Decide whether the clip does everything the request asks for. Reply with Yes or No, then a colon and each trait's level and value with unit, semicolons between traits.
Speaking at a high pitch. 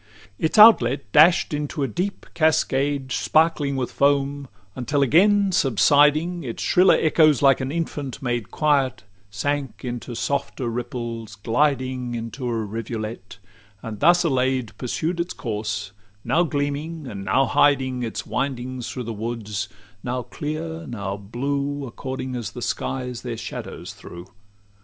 No: low, 130 Hz